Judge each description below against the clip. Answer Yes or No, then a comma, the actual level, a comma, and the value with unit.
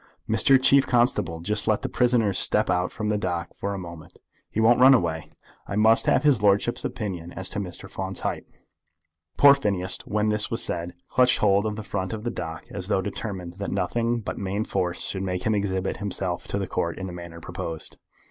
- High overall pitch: No, low, 100 Hz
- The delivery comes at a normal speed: No, fast, 210 wpm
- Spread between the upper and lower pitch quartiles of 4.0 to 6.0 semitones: No, average, 3.4 semitones